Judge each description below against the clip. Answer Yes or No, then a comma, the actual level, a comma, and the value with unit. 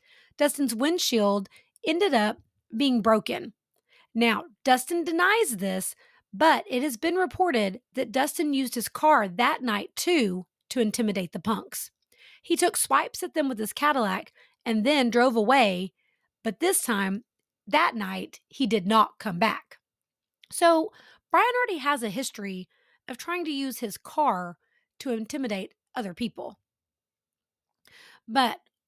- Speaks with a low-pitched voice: No, very high, 255 Hz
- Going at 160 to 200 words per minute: No, slow, 135 wpm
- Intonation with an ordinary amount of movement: No, wide, 6.4 semitones